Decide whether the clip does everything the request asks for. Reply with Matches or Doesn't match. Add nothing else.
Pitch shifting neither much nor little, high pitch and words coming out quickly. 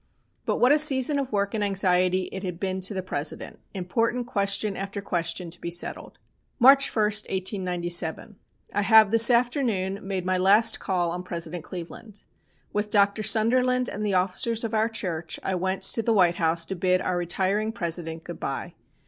Doesn't match